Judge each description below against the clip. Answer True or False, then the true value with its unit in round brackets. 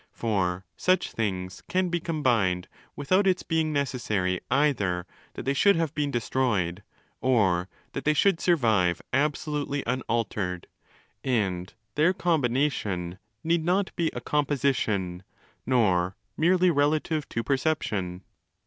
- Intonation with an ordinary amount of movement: False (8.5 semitones)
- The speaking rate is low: True (120 wpm)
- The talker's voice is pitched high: False (130 Hz)